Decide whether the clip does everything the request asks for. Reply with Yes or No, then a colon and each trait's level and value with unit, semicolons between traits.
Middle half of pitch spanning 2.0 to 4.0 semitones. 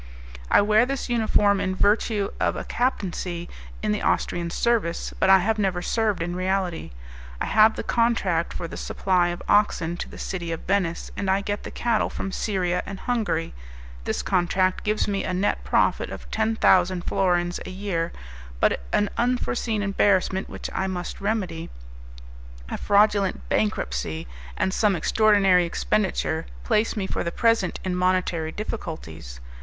Yes: average, 3.3 semitones